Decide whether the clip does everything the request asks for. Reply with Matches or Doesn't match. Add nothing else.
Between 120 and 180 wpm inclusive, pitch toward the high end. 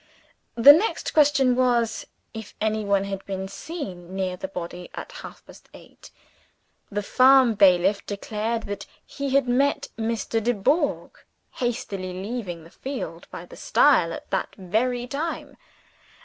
Matches